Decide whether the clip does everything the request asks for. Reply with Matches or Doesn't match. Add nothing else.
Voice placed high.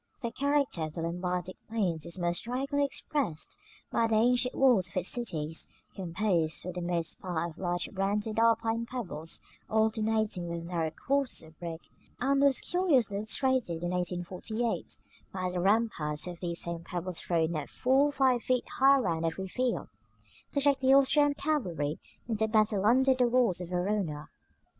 Matches